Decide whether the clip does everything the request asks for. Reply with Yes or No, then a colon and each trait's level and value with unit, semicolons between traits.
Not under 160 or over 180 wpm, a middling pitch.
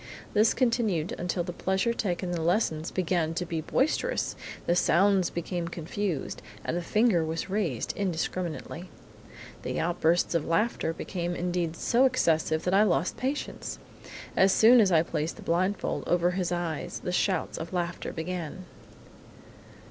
No: average, 150 wpm; medium, 175 Hz